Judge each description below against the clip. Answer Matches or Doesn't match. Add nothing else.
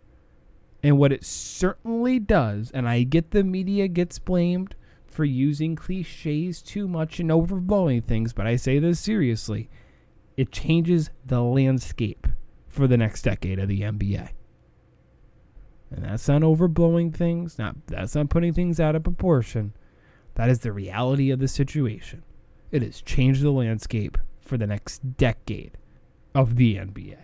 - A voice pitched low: Matches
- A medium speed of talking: Matches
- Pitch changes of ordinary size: Doesn't match